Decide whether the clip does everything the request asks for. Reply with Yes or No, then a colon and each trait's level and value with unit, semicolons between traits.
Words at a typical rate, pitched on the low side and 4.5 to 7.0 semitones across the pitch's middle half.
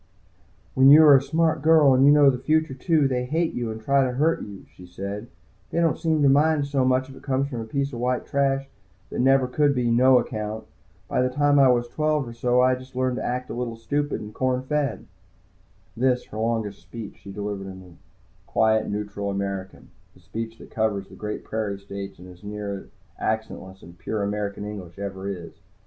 No: fast, 220 wpm; low, 125 Hz; average, 4.9 semitones